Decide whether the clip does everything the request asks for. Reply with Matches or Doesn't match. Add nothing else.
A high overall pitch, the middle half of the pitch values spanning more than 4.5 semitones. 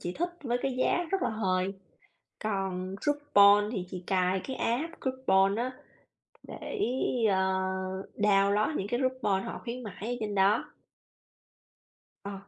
Matches